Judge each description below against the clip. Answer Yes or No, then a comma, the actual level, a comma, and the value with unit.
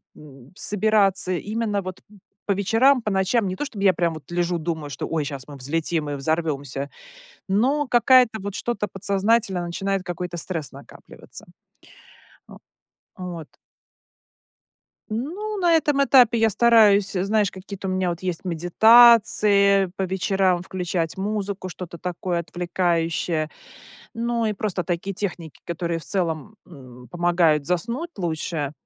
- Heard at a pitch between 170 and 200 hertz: Yes, medium, 185 Hz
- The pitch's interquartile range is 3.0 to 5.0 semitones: Yes, average, 4.0 semitones